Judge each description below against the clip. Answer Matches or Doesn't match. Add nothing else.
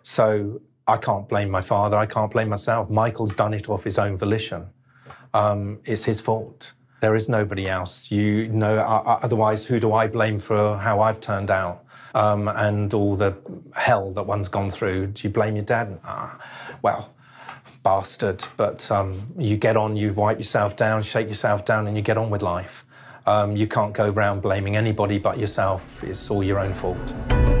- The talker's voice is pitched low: Matches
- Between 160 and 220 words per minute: Matches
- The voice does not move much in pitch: Matches